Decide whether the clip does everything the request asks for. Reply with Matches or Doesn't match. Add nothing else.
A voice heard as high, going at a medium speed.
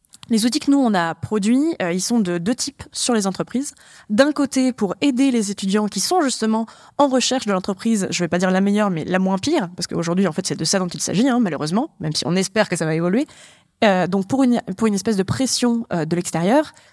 Doesn't match